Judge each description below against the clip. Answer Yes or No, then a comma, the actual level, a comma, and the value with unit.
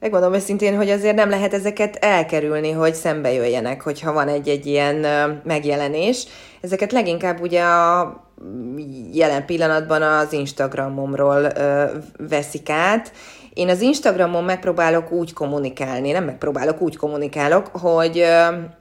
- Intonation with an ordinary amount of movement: Yes, average, 3.7 semitones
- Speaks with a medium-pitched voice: Yes, medium, 155 Hz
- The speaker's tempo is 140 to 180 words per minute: No, average, 120 wpm